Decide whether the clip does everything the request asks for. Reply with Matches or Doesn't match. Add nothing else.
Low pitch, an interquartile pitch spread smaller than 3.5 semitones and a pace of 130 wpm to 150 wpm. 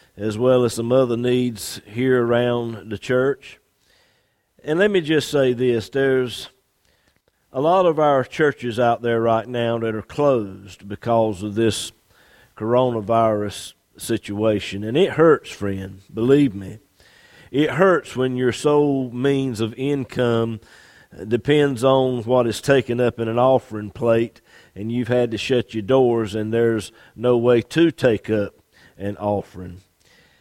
Matches